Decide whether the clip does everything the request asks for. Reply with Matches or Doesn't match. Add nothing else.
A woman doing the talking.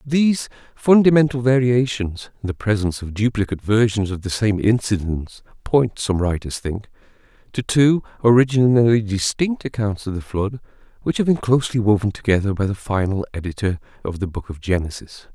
Doesn't match